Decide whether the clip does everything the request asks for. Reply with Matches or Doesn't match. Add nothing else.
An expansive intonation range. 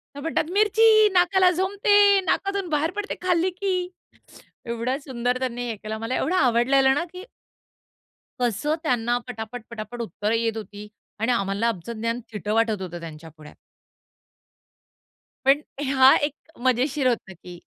Matches